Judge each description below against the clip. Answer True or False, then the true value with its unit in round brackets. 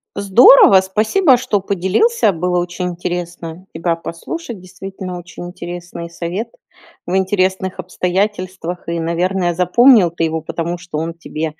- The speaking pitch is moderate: True (180 Hz)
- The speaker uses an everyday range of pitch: False (2.2 semitones)